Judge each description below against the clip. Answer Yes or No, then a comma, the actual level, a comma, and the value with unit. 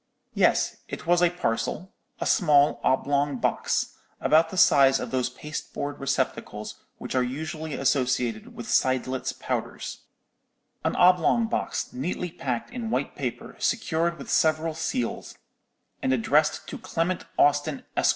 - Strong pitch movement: No, average, 4.3 semitones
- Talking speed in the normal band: No, slow, 125 wpm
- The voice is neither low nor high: Yes, medium, 145 Hz